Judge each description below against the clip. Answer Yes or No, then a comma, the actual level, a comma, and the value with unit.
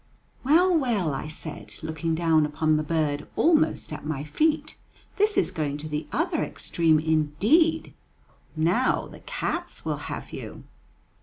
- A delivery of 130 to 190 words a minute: Yes, average, 145 wpm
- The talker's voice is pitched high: No, medium, 160 Hz